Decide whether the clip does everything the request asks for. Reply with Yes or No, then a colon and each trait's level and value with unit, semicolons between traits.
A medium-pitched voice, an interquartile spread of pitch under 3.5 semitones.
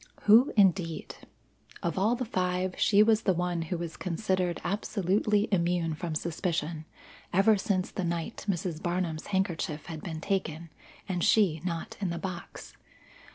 Yes: medium, 180 Hz; average, 2.9 semitones